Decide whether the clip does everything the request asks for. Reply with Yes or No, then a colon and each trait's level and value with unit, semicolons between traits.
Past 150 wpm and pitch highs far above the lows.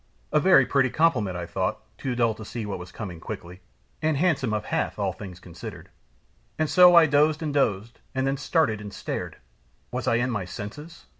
Yes: average, 200 wpm; wide, 7.0 semitones